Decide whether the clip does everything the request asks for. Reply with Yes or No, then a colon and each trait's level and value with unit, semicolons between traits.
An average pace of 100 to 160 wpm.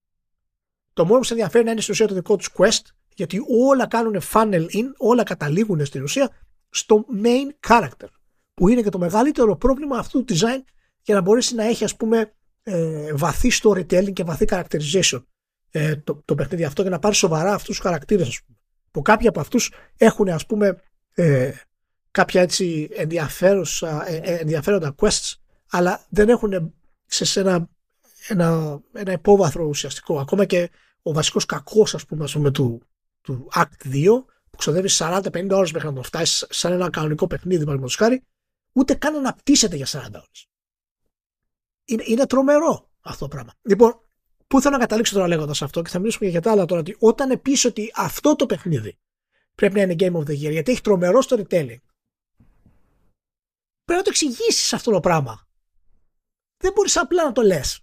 No: fast, 170 wpm